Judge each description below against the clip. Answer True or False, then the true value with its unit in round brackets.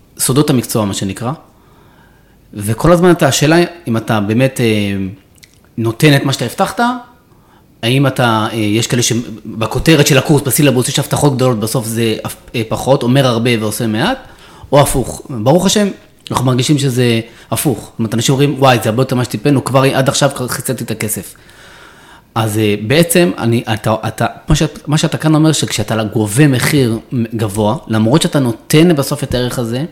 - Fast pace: True (175 wpm)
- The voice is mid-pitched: False (125 Hz)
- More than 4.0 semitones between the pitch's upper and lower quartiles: True (4.4 semitones)